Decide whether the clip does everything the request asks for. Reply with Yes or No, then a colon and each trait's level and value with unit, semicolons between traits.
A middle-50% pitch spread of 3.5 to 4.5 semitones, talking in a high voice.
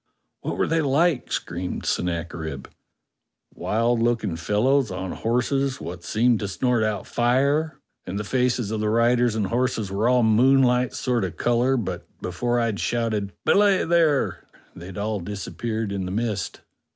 No: average, 4.0 semitones; low, 115 Hz